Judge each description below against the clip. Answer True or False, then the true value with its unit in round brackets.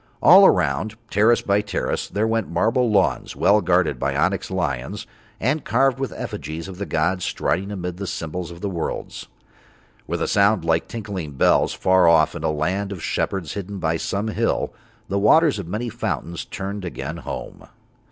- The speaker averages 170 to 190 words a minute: True (180 wpm)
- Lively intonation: False (3.8 semitones)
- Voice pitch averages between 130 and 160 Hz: False (95 Hz)